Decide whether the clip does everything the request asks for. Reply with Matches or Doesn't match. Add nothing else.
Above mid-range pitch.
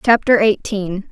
Matches